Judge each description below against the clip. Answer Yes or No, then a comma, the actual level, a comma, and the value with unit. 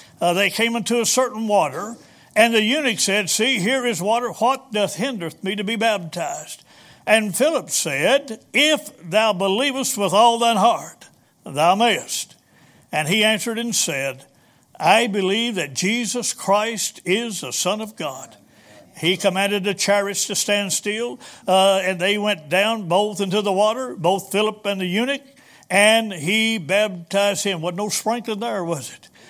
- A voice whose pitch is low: No, high, 210 Hz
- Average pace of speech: Yes, average, 165 wpm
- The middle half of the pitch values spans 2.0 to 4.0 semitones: Yes, average, 3.0 semitones